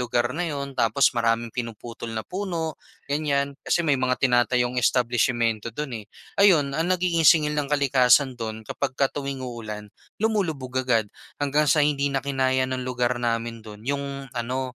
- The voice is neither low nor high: No, low, 130 Hz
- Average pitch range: Yes, average, 3.3 semitones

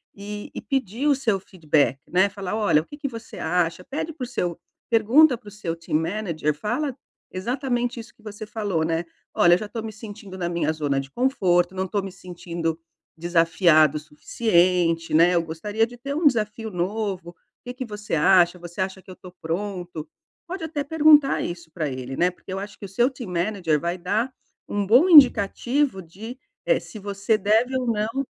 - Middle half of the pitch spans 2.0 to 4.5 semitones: No, average, 5.3 semitones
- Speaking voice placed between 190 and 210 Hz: Yes, high, 200 Hz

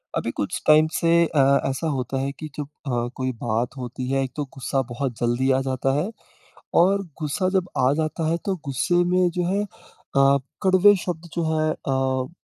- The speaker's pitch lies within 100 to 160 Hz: Yes, medium, 140 Hz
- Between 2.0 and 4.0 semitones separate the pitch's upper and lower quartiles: No, average, 4.4 semitones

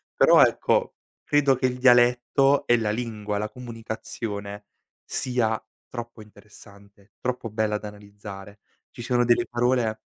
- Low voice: Yes, low, 115 Hz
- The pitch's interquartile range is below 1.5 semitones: No, average, 2.8 semitones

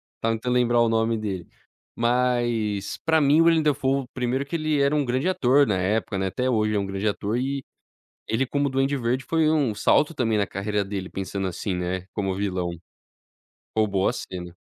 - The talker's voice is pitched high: No, low, 115 Hz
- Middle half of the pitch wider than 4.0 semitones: Yes, average, 5.2 semitones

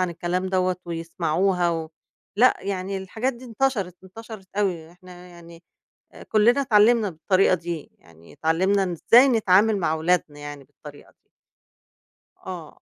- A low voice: No, medium, 185 Hz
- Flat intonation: No, average, 3.6 semitones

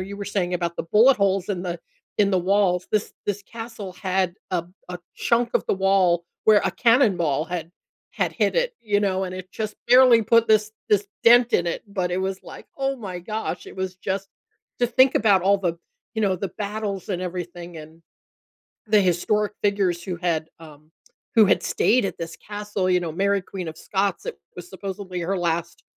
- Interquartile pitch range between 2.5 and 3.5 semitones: Yes, average, 2.9 semitones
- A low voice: No, high, 190 Hz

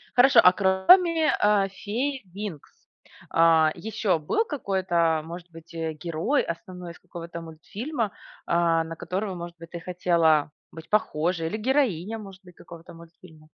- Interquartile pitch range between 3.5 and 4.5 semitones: Yes, average, 4.2 semitones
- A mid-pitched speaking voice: Yes, medium, 180 Hz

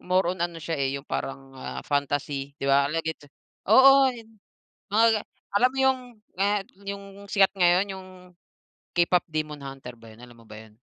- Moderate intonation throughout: No, wide, 6.4 semitones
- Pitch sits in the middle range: Yes, medium, 170 Hz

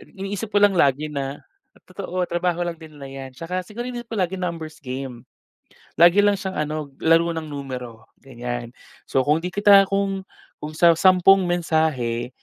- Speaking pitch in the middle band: Yes, medium, 165 Hz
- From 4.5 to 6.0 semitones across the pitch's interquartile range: Yes, wide, 5.5 semitones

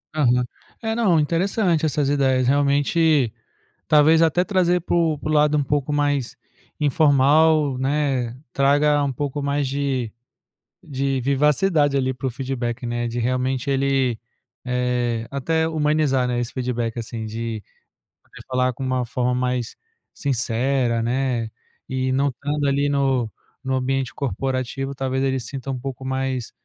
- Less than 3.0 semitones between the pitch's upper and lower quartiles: Yes, narrow, 2.6 semitones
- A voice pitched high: No, low, 135 Hz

